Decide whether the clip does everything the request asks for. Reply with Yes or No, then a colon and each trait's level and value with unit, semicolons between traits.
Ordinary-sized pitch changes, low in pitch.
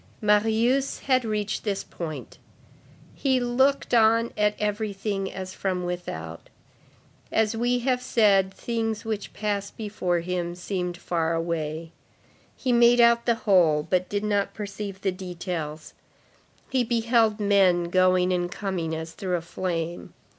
No: average, 4.1 semitones; high, 200 Hz